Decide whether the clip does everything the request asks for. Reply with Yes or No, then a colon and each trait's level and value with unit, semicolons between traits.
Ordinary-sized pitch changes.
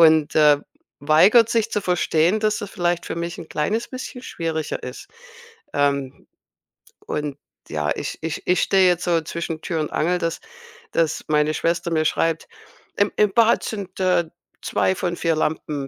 Yes: average, 3.4 semitones